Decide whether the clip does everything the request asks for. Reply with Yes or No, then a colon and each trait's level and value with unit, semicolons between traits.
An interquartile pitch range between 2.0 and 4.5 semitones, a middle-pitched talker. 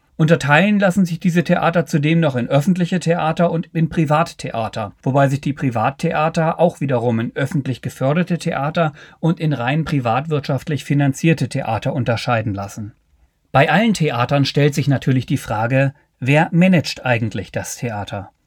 Yes: average, 4.1 semitones; medium, 145 Hz